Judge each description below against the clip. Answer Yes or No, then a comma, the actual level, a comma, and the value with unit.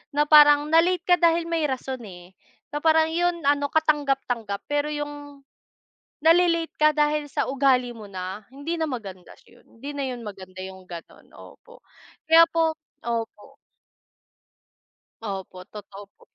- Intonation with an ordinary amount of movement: No, wide, 6.7 semitones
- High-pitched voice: Yes, very high, 285 Hz